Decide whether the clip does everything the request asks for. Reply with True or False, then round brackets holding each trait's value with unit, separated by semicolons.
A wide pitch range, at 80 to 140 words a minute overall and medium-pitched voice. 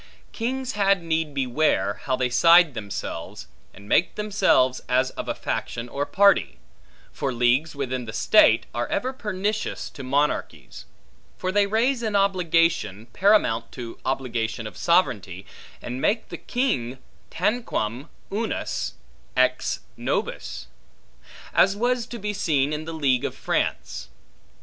True (8.6 semitones; 135 wpm; 155 Hz)